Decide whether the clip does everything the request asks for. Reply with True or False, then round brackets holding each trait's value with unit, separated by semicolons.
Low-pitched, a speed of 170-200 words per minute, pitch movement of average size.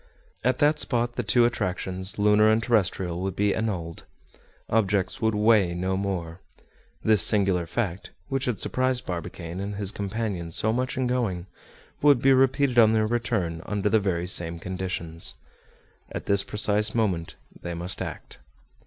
False (105 Hz; 155 wpm; 4.2 semitones)